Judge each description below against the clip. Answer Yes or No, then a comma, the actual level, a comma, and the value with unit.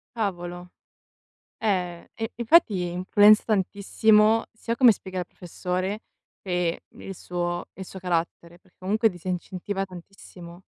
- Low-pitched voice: No, medium, 185 Hz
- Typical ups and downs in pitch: Yes, average, 3.1 semitones